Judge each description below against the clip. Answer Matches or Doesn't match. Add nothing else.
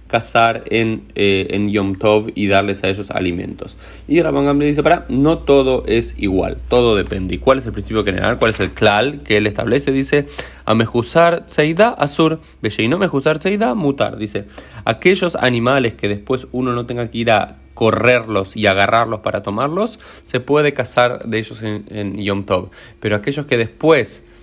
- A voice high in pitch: Doesn't match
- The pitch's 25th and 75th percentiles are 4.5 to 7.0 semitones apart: Matches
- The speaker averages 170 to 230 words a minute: Matches